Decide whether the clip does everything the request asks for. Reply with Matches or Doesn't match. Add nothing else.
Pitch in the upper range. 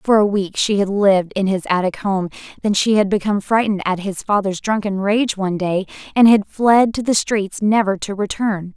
Matches